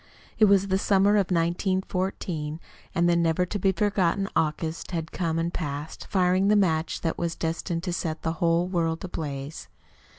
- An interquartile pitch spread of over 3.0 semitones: No, narrow, 2.6 semitones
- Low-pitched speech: No, medium, 170 Hz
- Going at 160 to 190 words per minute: Yes, average, 170 wpm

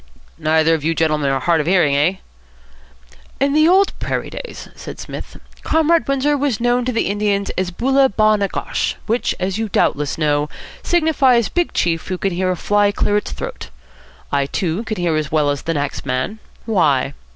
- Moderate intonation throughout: No, wide, 7.6 semitones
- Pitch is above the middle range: Yes, high, 195 Hz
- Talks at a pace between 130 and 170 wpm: No, average, 190 wpm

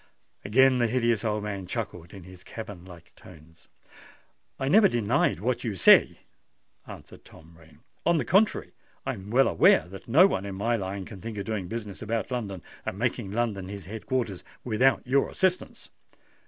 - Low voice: Yes, low, 105 Hz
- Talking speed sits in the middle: Yes, average, 180 wpm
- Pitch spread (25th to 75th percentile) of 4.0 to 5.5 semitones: Yes, average, 4.3 semitones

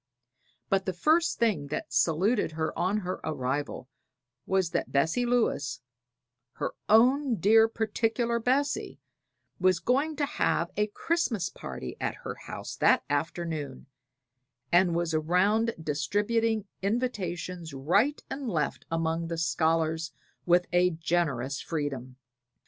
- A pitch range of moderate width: No, wide, 6.0 semitones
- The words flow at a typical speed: No, slow, 120 wpm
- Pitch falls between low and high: Yes, medium, 180 Hz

